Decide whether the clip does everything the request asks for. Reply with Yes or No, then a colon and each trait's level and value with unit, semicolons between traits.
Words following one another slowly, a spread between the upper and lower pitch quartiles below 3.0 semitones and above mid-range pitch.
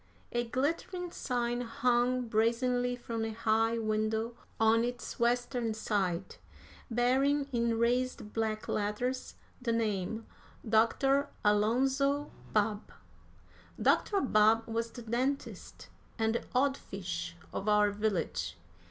Yes: slow, 110 wpm; narrow, 2.4 semitones; high, 230 Hz